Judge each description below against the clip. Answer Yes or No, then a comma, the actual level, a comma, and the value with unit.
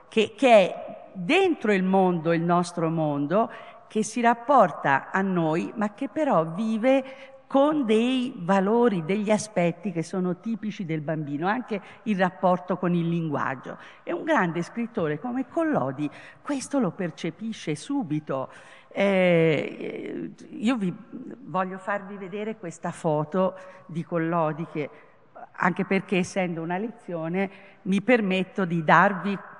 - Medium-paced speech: Yes, average, 130 wpm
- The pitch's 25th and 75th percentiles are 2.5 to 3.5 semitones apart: No, average, 4.9 semitones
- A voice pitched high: Yes, high, 195 Hz